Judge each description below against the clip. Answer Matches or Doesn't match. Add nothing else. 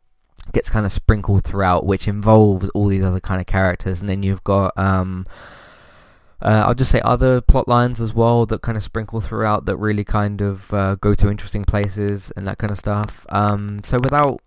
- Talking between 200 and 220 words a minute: Matches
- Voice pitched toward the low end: Matches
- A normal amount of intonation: Doesn't match